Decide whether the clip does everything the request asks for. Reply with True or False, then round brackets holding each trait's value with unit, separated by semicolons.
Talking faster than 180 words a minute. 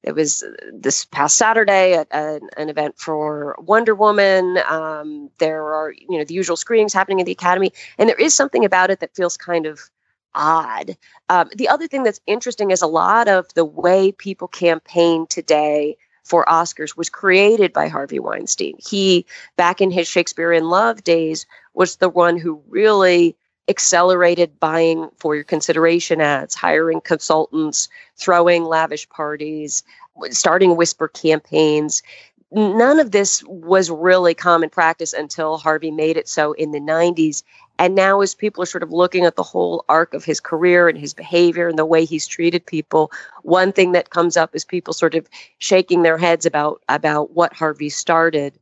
False (170 wpm)